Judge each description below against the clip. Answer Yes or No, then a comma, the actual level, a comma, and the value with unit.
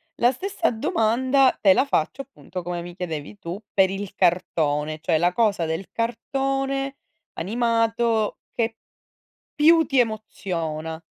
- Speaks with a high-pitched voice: Yes, high, 215 Hz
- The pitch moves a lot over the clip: Yes, wide, 6.9 semitones